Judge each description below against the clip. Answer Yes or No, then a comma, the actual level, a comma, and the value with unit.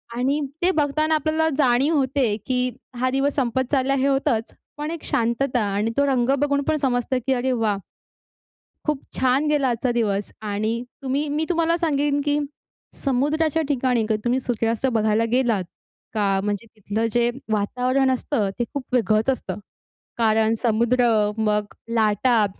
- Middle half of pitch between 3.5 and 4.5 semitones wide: Yes, average, 3.9 semitones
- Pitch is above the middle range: Yes, very high, 255 Hz